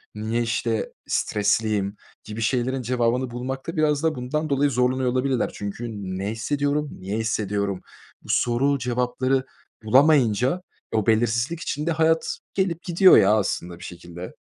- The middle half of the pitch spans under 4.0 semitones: No, average, 4.5 semitones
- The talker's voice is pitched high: No, low, 125 Hz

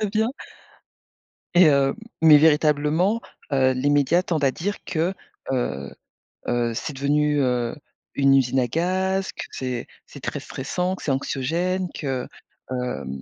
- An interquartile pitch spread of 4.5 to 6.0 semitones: Yes, average, 5.2 semitones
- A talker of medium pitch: Yes, medium, 145 Hz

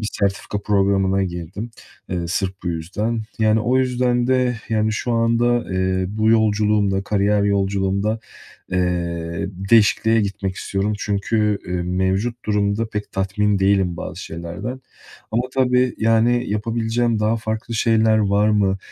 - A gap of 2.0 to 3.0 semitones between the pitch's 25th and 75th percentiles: Yes, average, 2.7 semitones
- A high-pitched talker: No, low, 105 Hz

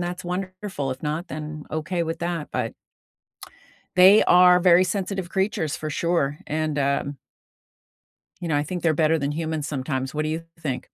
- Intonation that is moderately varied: Yes, average, 3.1 semitones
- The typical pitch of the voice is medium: Yes, medium, 160 Hz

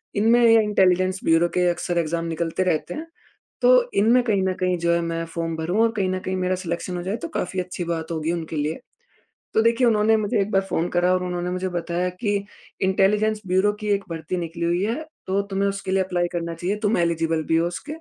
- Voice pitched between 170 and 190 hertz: Yes, medium, 185 Hz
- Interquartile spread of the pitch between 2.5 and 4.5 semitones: Yes, average, 3.3 semitones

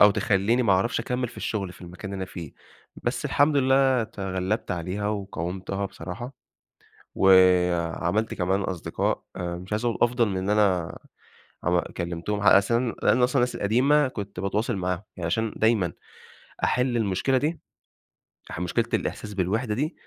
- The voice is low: Yes, low, 100 Hz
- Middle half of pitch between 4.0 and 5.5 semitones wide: Yes, average, 4.4 semitones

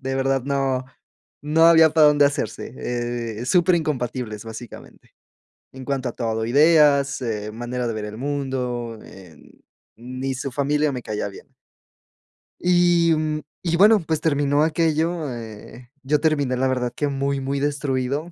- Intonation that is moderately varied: Yes, average, 3.7 semitones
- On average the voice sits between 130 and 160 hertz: Yes, medium, 140 Hz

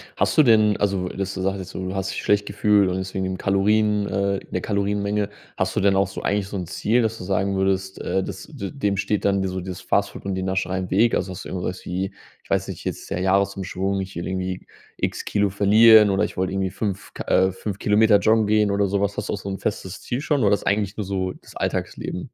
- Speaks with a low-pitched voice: Yes, low, 100 Hz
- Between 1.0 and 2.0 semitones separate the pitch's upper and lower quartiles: Yes, narrow, 1.5 semitones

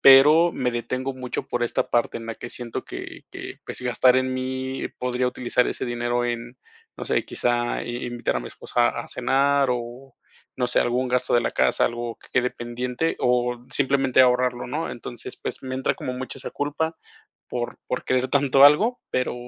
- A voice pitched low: Yes, low, 125 Hz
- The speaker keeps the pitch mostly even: Yes, narrow, 1.6 semitones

